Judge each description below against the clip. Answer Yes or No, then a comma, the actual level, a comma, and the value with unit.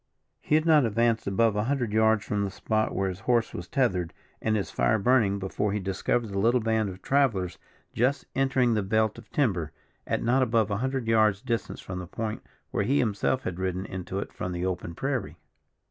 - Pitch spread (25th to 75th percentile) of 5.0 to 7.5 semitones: No, average, 3.8 semitones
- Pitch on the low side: Yes, low, 110 Hz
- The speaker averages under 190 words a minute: No, fast, 205 wpm